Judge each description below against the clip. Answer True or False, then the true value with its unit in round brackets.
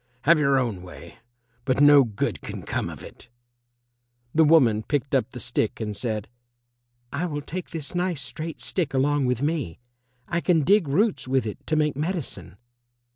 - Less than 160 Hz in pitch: True (140 Hz)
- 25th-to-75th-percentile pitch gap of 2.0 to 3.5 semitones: False (4.8 semitones)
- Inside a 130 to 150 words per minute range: False (175 wpm)